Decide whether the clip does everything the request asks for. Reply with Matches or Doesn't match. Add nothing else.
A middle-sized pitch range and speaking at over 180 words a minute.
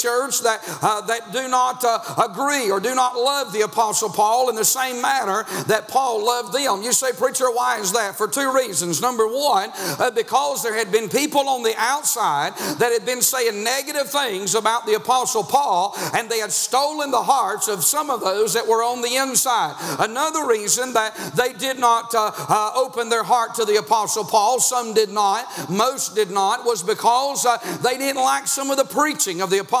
Matches